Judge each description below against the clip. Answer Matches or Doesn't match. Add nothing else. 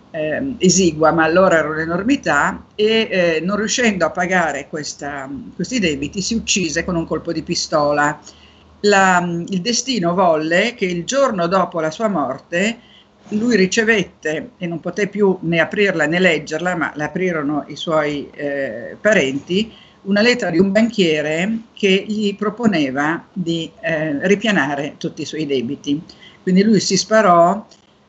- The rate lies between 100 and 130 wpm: Doesn't match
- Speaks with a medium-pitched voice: Matches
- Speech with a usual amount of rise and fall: Matches